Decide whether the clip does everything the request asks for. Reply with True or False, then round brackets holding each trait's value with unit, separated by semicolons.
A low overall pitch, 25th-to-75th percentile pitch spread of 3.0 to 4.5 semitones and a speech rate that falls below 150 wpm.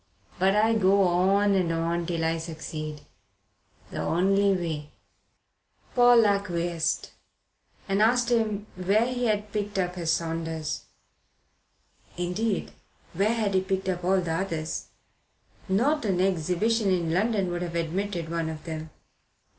False (185 Hz; 3.6 semitones; 135 wpm)